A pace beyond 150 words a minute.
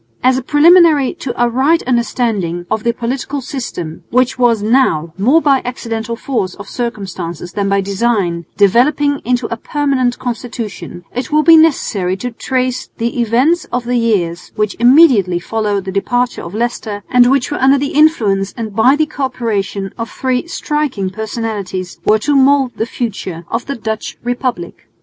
Yes: average, 165 wpm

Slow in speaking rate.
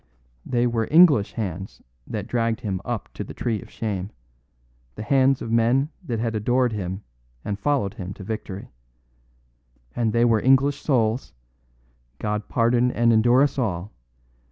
No: average, 155 wpm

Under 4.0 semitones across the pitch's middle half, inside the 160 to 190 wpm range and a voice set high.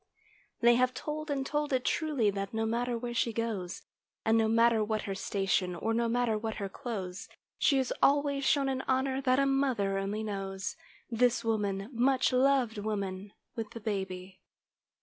No: average, 4.4 semitones; average, 175 wpm; high, 230 Hz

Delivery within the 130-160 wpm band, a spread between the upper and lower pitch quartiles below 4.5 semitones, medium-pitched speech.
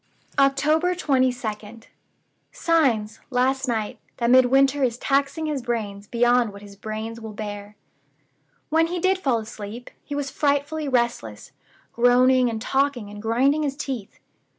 No: slow, 135 wpm; average, 4.1 semitones; very high, 250 Hz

